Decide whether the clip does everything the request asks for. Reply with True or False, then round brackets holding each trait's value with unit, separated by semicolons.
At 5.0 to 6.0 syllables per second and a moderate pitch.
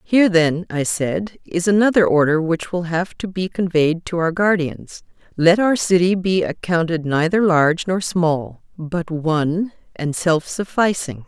False (4.2 syllables/s; 175 Hz)